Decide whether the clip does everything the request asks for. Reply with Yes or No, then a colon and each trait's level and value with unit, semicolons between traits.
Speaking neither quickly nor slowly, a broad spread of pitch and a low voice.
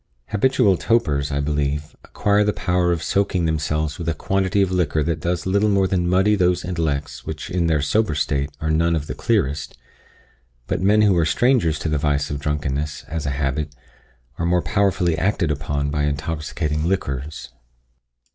No: average, 175 wpm; average, 4.1 semitones; very low, 80 Hz